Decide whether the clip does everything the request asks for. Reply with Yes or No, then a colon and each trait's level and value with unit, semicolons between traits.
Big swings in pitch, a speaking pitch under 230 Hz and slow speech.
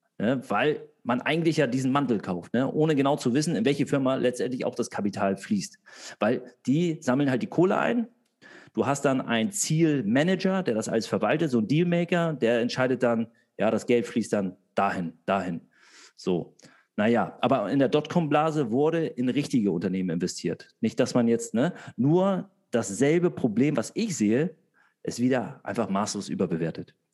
No: wide, 6.4 semitones; medium, 140 Hz; average, 170 wpm